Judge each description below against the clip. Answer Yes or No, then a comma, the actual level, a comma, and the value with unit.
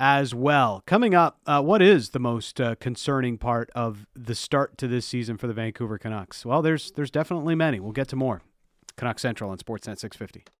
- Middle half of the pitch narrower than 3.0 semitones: No, average, 3.7 semitones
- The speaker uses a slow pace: No, fast, 205 wpm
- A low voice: Yes, low, 120 Hz